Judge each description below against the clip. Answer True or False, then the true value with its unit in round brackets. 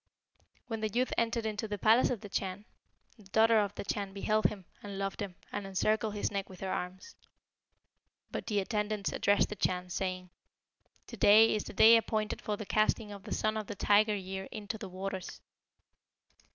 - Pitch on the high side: True (205 Hz)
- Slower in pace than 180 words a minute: False (190 wpm)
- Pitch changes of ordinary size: False (1.9 semitones)